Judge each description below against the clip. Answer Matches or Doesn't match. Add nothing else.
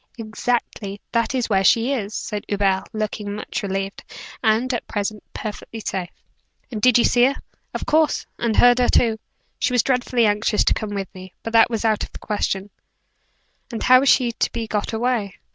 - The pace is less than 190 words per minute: Doesn't match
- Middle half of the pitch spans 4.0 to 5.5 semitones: Doesn't match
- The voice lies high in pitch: Matches